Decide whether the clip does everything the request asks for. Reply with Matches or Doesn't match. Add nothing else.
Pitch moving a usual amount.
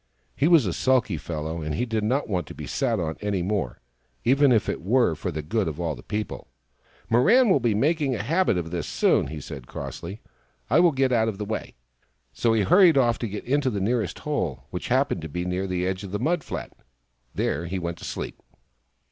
Doesn't match